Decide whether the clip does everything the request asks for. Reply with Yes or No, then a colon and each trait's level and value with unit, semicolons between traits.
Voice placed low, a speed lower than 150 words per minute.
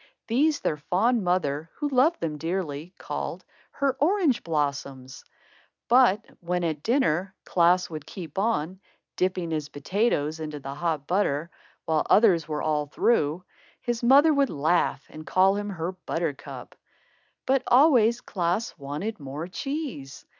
No: medium, 180 Hz; average, 140 wpm